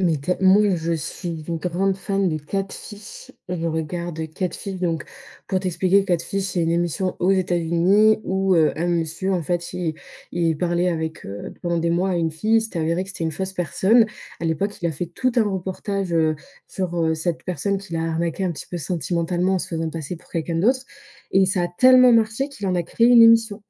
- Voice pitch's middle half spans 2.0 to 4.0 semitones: Yes, average, 2.8 semitones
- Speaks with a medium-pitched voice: Yes, medium, 180 Hz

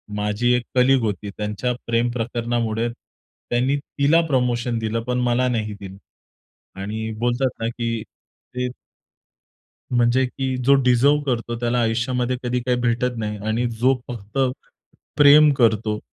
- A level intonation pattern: Yes, narrow, 1.8 semitones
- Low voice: Yes, low, 120 Hz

